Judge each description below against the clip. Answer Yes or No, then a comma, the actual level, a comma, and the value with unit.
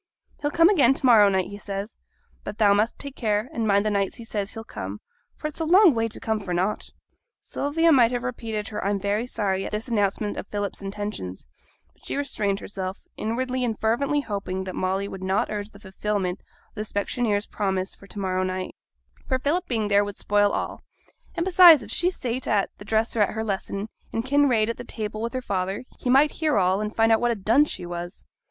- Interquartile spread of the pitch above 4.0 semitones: No, average, 3.7 semitones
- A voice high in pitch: Yes, high, 215 Hz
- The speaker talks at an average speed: No, fast, 220 wpm